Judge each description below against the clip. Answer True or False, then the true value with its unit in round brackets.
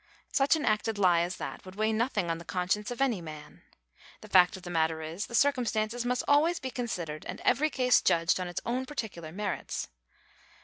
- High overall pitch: True (210 Hz)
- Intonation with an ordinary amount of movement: False (6.2 semitones)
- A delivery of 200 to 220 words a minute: True (205 wpm)